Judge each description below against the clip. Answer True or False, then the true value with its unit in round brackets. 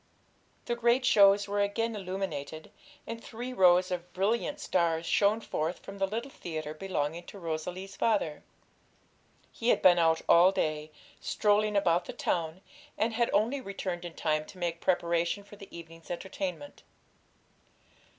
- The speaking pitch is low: False (190 Hz)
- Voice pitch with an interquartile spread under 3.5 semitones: False (4.0 semitones)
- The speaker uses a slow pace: False (150 wpm)